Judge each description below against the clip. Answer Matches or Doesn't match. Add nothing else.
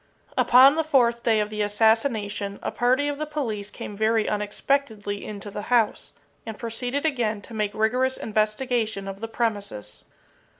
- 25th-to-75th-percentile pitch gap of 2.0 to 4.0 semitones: Matches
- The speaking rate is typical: Matches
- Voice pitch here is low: Doesn't match